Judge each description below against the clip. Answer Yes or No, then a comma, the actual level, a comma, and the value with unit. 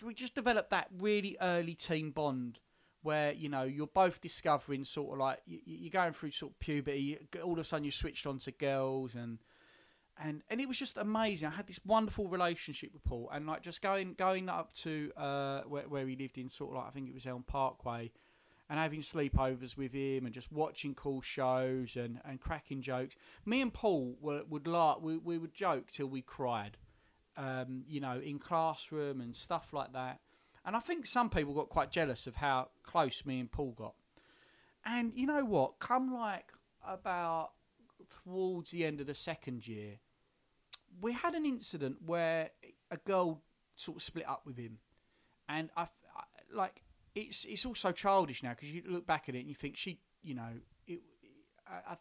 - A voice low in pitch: No, medium, 150 Hz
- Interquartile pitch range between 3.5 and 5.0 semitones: No, wide, 5.6 semitones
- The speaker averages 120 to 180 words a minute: No, average, 195 wpm